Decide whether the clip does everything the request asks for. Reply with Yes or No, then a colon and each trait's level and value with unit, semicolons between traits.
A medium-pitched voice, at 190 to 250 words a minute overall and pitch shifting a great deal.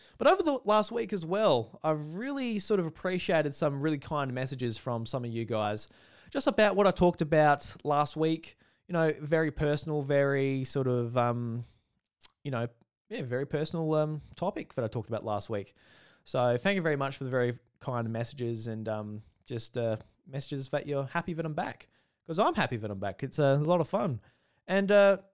Yes: medium, 145 Hz; average, 200 wpm; wide, 6.2 semitones